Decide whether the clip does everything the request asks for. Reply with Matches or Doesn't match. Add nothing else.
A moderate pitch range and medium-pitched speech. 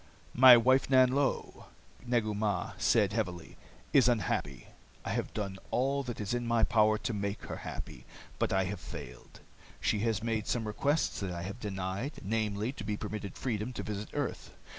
Doesn't match